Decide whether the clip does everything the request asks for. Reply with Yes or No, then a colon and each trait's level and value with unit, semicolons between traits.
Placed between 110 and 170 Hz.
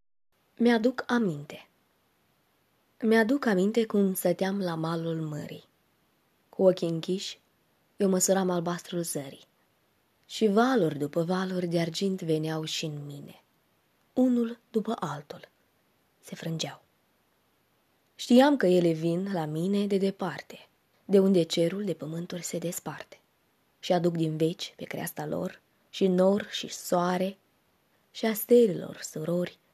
No: medium, 180 Hz